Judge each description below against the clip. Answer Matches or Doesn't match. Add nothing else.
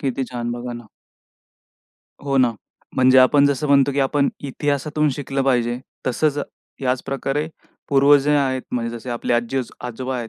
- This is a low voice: Matches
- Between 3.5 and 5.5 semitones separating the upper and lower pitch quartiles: Doesn't match